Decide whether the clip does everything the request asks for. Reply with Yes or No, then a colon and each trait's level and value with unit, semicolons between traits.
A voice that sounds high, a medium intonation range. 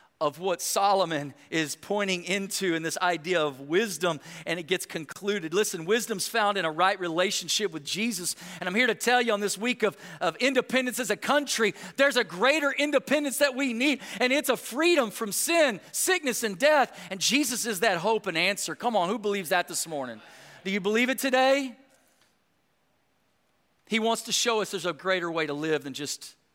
No: high, 205 Hz; wide, 6.0 semitones